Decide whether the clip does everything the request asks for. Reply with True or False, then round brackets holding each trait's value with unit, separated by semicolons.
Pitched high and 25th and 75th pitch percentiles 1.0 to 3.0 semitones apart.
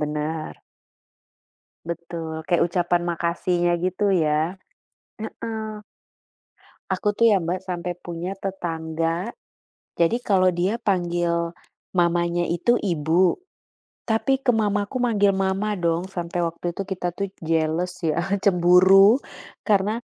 False (175 Hz; 2.6 semitones)